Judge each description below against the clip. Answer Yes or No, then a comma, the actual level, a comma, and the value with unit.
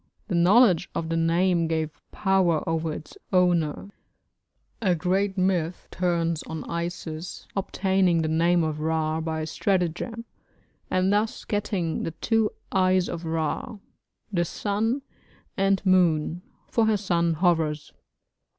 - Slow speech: Yes, slow, 125 wpm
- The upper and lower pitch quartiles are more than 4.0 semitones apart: No, average, 2.9 semitones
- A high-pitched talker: No, medium, 175 Hz